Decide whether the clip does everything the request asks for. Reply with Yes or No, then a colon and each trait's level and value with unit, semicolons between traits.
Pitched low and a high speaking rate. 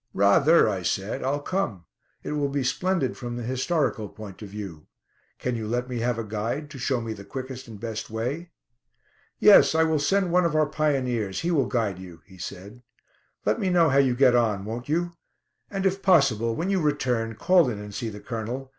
Yes: low, 125 Hz; fast, 210 wpm